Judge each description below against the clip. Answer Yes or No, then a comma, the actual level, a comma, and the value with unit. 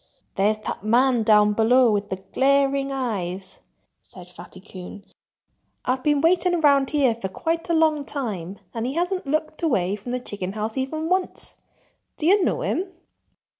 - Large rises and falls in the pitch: Yes, wide, 6.8 semitones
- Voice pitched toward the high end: Yes, very high, 255 Hz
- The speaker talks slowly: No, average, 165 wpm